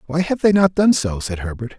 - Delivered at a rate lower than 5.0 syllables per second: No, 5.5 syllables/s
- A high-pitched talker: No, medium, 145 Hz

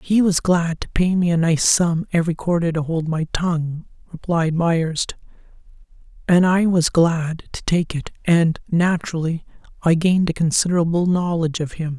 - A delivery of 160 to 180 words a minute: Yes, average, 165 wpm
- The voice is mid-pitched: Yes, medium, 170 Hz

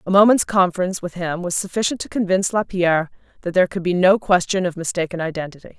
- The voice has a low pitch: No, medium, 180 Hz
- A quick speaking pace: No, average, 195 wpm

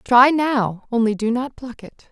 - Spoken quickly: No, average, 170 wpm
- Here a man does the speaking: No, female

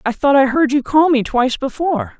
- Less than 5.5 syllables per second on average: No, 5.8 syllables/s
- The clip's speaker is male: No, female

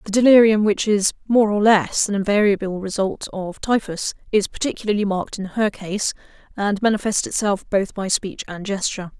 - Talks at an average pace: Yes, average, 170 wpm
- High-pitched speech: Yes, high, 205 Hz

